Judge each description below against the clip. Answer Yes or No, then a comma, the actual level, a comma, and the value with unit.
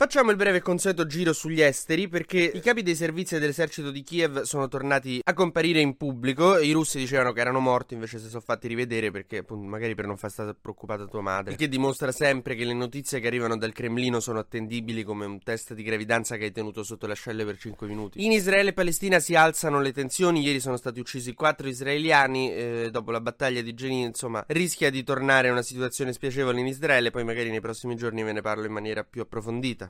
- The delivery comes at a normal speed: No, fast, 225 wpm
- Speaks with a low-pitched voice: Yes, low, 125 Hz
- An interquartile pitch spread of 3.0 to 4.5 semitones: No, average, 5.0 semitones